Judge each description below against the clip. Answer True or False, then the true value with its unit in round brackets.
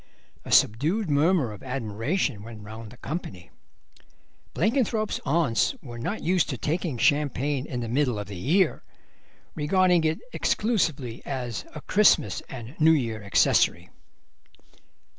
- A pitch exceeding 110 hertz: True (140 Hz)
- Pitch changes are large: True (6.7 semitones)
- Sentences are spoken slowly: True (130 wpm)